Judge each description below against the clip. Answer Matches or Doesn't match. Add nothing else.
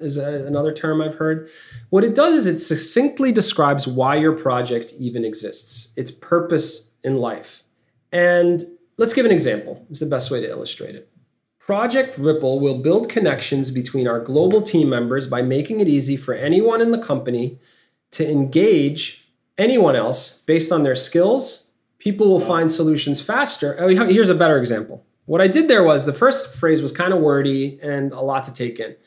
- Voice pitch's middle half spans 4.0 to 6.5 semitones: Matches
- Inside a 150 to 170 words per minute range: Doesn't match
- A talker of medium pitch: Matches